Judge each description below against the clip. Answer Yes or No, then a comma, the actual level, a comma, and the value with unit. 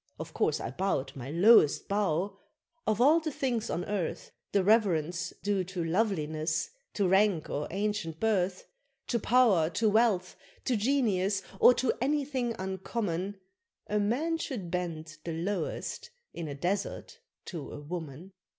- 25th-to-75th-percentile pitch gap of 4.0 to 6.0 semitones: Yes, average, 4.9 semitones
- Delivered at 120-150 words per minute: Yes, average, 145 wpm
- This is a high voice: Yes, high, 195 Hz